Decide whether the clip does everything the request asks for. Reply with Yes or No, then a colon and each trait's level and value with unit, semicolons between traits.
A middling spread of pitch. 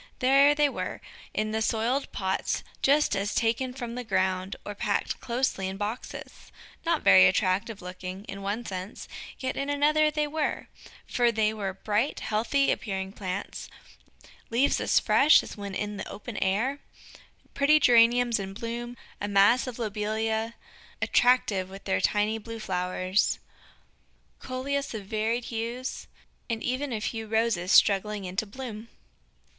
Yes: average, 4.0 semitones